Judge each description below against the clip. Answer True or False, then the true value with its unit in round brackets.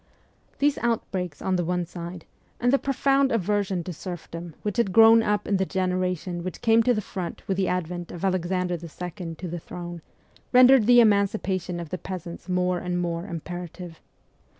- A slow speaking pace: False (175 wpm)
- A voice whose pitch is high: False (180 Hz)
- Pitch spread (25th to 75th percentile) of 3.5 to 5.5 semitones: False (3.1 semitones)